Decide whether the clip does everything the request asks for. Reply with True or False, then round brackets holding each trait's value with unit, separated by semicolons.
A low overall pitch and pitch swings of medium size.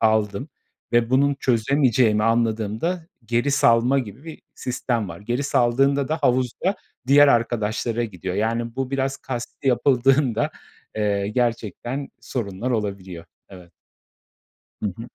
True (120 Hz; 3.7 semitones)